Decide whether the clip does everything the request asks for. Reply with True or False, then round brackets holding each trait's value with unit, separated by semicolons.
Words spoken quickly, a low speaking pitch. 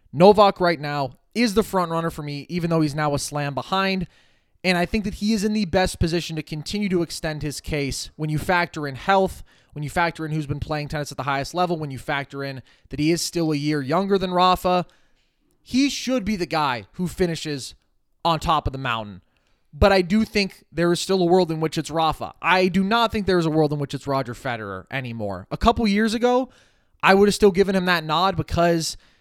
False (235 wpm; 165 Hz)